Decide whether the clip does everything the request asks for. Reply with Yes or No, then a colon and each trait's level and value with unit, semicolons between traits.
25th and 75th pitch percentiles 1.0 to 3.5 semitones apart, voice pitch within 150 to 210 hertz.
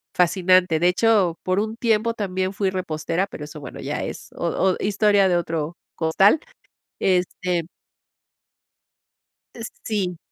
Yes: average, 2.9 semitones; medium, 185 Hz